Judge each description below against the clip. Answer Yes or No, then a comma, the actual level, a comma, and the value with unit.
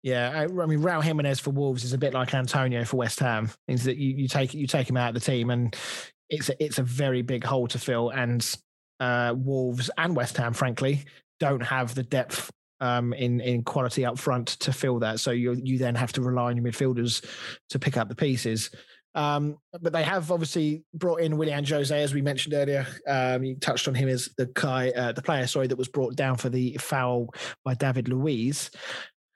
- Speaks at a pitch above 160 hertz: No, low, 130 Hz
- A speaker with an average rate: No, fast, 220 wpm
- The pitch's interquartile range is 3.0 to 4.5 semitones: No, narrow, 2.6 semitones